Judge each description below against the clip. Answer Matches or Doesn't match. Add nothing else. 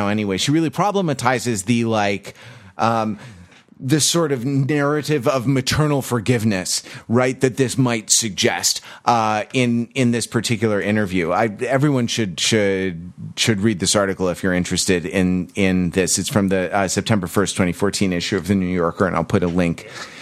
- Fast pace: Doesn't match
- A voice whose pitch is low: Matches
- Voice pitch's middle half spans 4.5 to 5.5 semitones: Matches